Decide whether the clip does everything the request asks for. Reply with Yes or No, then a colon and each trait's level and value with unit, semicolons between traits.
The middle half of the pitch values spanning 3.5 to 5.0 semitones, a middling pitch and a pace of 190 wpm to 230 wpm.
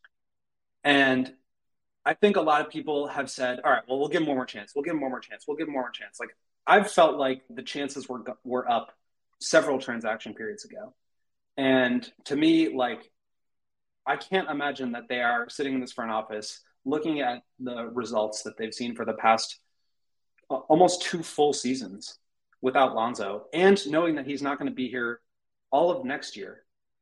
No: average, 4.0 semitones; low, 130 Hz; average, 200 wpm